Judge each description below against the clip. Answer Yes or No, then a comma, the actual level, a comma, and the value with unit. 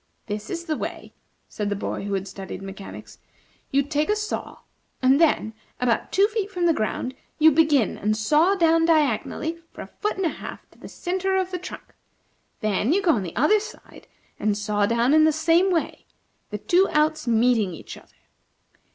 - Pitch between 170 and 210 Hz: No, very high, 300 Hz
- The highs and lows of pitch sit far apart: Yes, wide, 8.2 semitones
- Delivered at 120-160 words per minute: No, average, 195 wpm